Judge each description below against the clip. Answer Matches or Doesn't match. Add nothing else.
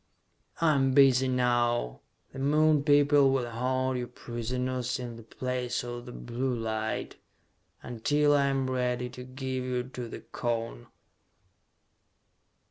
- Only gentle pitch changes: Matches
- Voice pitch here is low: Matches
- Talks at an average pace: Doesn't match